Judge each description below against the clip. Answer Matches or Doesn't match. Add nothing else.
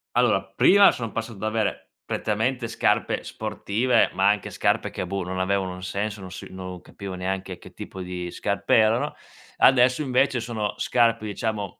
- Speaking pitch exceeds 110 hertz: Doesn't match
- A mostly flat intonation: Doesn't match